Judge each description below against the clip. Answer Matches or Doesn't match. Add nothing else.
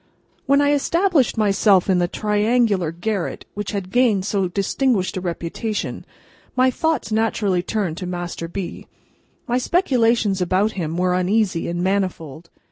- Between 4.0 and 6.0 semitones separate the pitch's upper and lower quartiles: Matches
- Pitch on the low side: Doesn't match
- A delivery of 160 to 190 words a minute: Doesn't match